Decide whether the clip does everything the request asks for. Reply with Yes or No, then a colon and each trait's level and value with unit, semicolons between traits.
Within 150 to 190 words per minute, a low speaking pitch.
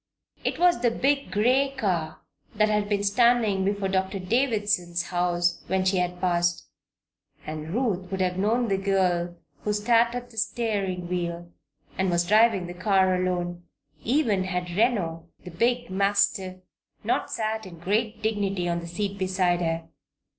No: average, 155 wpm; high, 190 Hz